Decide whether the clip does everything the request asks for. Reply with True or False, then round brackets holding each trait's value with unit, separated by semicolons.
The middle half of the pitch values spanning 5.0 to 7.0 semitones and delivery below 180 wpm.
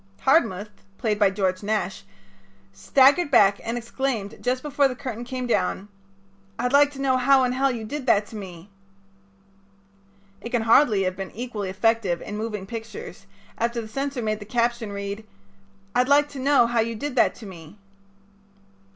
False (4.1 semitones; 170 wpm)